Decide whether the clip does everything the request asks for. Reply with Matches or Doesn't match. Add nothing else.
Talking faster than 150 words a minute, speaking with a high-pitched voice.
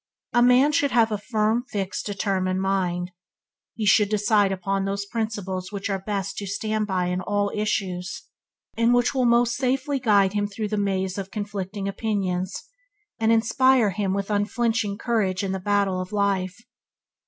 Matches